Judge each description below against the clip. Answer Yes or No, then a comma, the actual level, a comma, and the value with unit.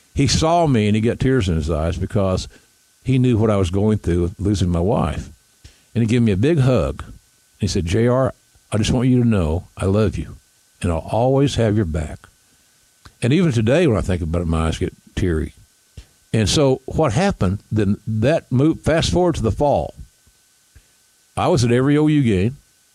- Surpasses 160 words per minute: Yes, average, 200 wpm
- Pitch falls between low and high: No, low, 110 Hz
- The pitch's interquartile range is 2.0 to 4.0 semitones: No, wide, 5.5 semitones